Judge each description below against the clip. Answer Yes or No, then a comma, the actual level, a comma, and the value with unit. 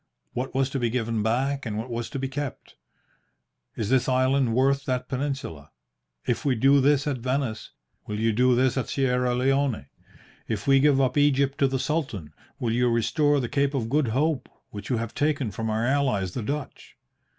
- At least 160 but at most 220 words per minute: Yes, average, 195 wpm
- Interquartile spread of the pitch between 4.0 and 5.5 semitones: No, average, 3.1 semitones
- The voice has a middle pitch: No, low, 130 Hz